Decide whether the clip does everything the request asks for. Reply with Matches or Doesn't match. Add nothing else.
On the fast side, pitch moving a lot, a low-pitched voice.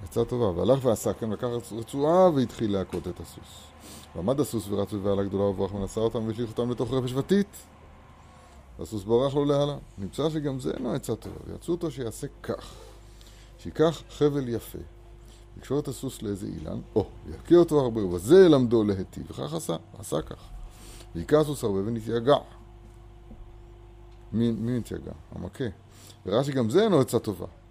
Doesn't match